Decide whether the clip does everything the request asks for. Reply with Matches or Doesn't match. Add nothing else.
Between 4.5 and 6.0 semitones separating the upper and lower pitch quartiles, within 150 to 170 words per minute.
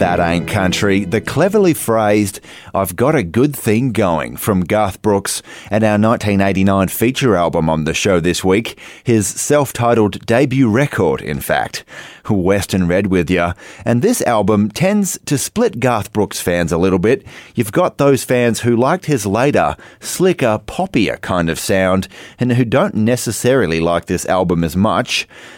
Matches